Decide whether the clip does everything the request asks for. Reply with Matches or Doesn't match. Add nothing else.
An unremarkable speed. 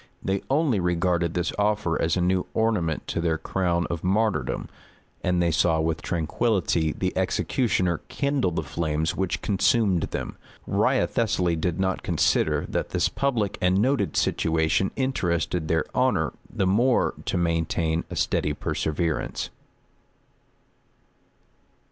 Doesn't match